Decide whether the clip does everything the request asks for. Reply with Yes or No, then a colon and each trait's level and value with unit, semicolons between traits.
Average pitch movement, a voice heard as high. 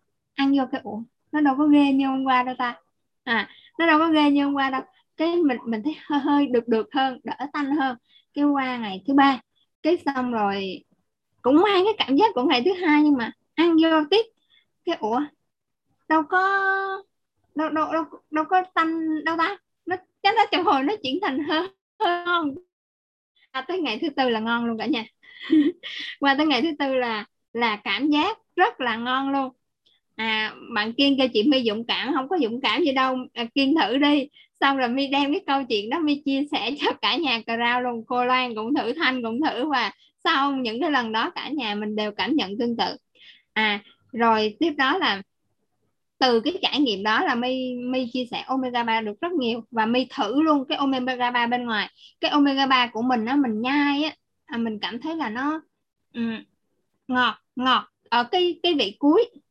Yes: average, 4.6 semitones; very high, 275 Hz